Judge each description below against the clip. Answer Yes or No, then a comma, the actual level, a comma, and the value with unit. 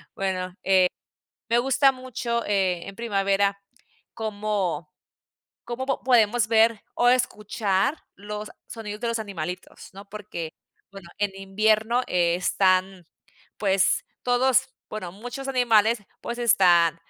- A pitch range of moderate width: Yes, average, 3.5 semitones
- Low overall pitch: No, high, 210 Hz